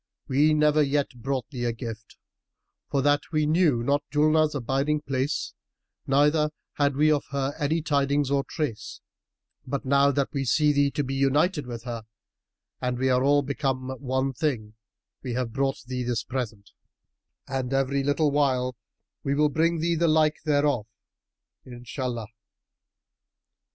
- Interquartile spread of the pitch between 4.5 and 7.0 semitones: No, narrow, 2.6 semitones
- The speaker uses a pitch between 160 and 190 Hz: No, medium, 140 Hz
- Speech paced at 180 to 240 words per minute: No, average, 150 wpm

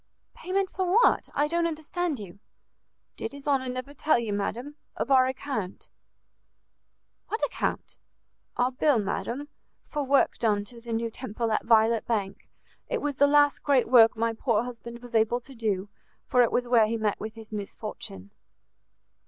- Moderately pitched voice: No, high, 240 Hz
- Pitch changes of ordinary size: Yes, average, 4.4 semitones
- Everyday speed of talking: Yes, average, 170 wpm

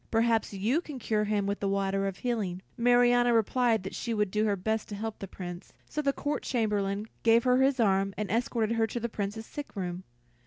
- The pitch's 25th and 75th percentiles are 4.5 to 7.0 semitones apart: No, average, 3.3 semitones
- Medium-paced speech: No, fast, 220 wpm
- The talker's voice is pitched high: Yes, high, 220 Hz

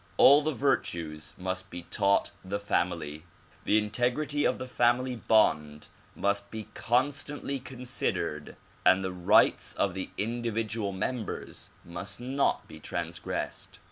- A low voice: Yes, low, 105 Hz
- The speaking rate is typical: No, slow, 130 wpm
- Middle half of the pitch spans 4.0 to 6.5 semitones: Yes, average, 5.2 semitones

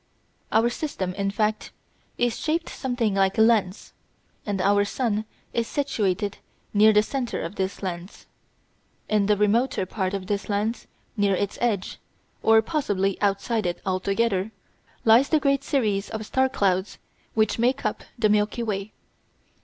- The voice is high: Yes, high, 210 Hz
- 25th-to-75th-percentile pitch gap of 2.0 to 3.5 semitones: Yes, average, 2.9 semitones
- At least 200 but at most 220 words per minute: No, average, 150 wpm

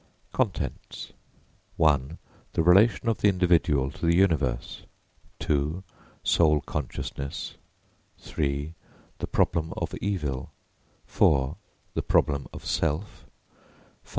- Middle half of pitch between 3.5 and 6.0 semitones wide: Yes, average, 4.0 semitones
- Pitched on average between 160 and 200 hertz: No, very low, 75 Hz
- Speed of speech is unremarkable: No, slow, 100 wpm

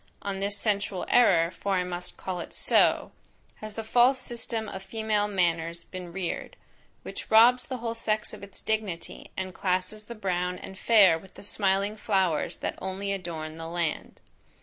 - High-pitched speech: Yes, high, 195 Hz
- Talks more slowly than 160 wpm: No, average, 170 wpm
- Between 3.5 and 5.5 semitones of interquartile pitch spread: No, average, 3.1 semitones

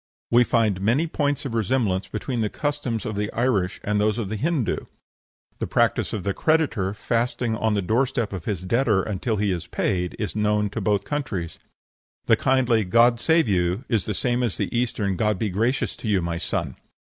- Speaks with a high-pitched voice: No, low, 110 Hz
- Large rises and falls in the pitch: No, average, 3.7 semitones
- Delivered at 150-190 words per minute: No, average, 200 wpm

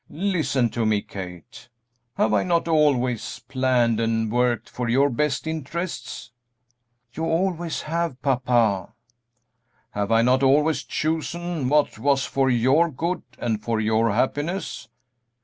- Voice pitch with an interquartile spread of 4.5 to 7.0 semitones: Yes, wide, 5.6 semitones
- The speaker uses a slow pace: Yes, slow, 130 wpm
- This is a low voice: Yes, low, 130 Hz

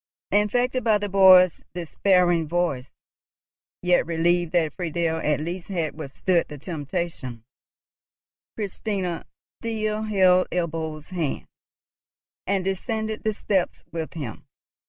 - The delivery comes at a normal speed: No, slow, 110 wpm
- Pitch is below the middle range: No, medium, 175 Hz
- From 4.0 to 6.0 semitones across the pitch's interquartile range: No, average, 3.4 semitones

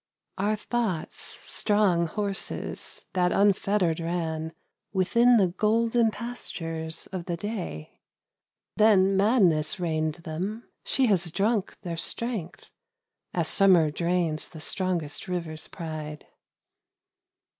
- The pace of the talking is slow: Yes, slow, 100 wpm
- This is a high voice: No, medium, 180 Hz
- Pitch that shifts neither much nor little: Yes, average, 4.3 semitones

